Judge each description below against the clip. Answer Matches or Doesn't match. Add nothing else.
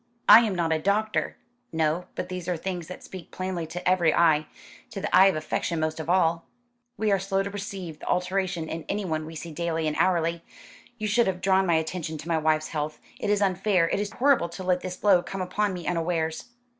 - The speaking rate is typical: Doesn't match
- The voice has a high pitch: Doesn't match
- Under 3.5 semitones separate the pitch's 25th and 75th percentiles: Matches